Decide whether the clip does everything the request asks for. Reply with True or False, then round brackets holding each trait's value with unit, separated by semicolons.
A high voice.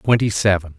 False (100 Hz)